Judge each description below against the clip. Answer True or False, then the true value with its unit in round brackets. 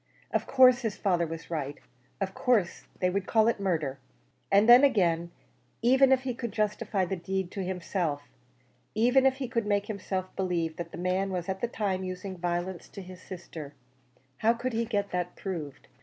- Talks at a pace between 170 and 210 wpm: True (185 wpm)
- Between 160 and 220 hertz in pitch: True (190 Hz)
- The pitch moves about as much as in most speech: True (4.3 semitones)